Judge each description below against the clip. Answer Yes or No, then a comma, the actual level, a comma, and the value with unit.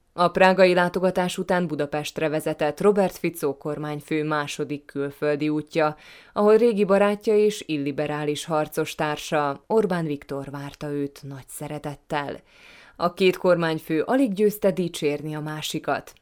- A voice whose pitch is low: No, medium, 155 Hz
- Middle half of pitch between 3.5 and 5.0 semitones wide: Yes, average, 3.8 semitones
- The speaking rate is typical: Yes, average, 120 wpm